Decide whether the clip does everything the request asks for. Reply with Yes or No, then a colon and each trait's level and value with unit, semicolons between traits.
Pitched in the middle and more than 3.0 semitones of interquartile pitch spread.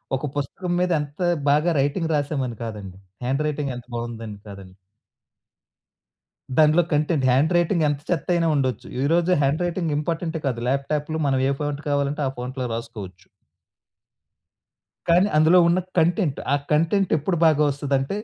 Yes: medium, 145 Hz; average, 3.9 semitones